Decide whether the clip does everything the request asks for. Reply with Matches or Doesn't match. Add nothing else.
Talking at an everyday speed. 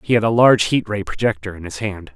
Doesn't match